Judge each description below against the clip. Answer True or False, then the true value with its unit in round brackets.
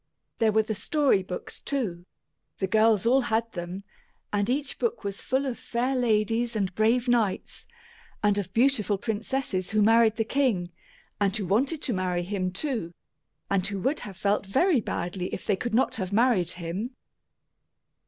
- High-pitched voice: True (215 Hz)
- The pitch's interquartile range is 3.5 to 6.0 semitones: True (4.3 semitones)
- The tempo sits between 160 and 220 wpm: True (170 wpm)